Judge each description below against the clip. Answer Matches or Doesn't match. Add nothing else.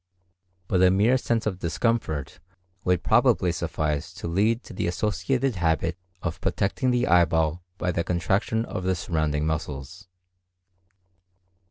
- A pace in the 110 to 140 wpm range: Matches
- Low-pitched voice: Matches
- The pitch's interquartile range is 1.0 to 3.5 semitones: Doesn't match